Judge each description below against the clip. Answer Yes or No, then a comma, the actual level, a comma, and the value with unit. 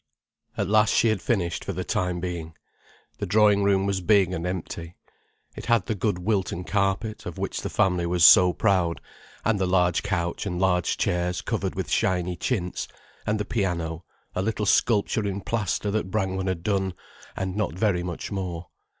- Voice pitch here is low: Yes, very low, 95 Hz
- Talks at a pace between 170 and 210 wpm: Yes, average, 180 wpm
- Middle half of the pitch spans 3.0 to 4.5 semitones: No, narrow, 2.6 semitones